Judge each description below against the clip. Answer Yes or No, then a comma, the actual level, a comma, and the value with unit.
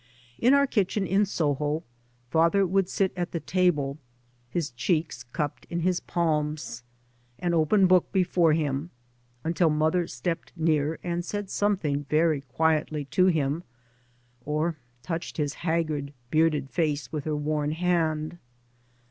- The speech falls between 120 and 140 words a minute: Yes, slow, 135 wpm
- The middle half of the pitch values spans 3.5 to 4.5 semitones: No, average, 3.0 semitones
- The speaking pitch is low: No, medium, 160 Hz